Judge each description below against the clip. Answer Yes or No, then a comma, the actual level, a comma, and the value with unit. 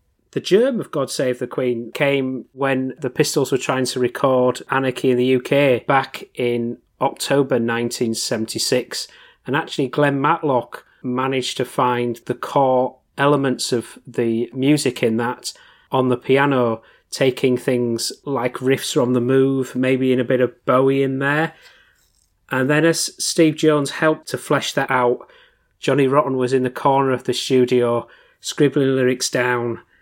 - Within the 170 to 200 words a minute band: No, average, 155 wpm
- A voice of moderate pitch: No, low, 130 Hz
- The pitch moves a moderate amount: No, narrow, 2.0 semitones